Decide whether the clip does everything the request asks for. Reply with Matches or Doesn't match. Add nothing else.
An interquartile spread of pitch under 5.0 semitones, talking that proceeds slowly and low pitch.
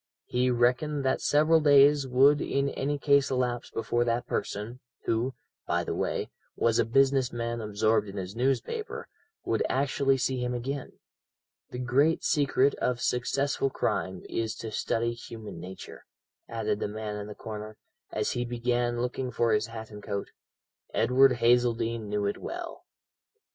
Doesn't match